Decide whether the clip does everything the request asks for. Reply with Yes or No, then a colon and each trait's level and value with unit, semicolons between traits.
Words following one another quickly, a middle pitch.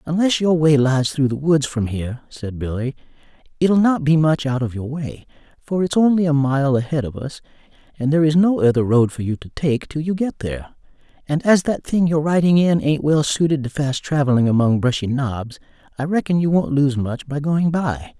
Yes: fast, 220 wpm; medium, 145 Hz